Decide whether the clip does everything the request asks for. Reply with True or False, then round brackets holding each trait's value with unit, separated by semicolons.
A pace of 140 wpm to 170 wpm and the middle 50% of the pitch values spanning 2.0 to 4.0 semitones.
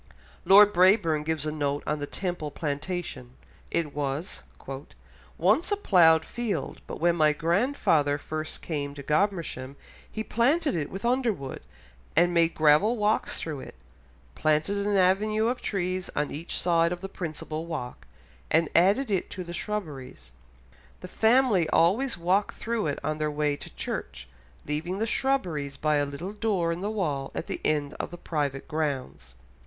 False (160 wpm; 5.2 semitones)